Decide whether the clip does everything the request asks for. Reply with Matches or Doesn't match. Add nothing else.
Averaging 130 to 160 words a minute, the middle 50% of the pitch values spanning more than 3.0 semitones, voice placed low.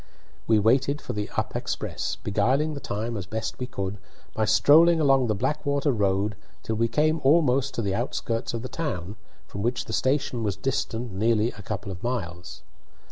Doesn't match